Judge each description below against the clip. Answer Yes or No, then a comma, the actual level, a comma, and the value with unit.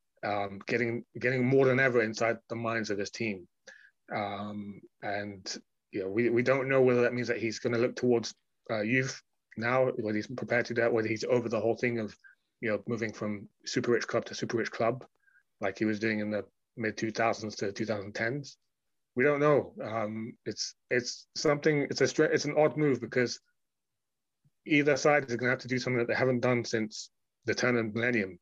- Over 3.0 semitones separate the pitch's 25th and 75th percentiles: No, average, 2.7 semitones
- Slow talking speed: No, fast, 205 wpm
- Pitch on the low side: Yes, low, 115 Hz